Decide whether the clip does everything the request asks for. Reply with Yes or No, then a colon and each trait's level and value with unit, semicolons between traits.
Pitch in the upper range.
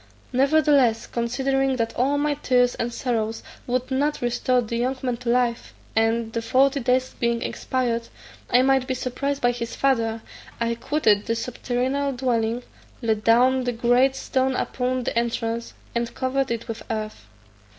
Yes: high, 245 Hz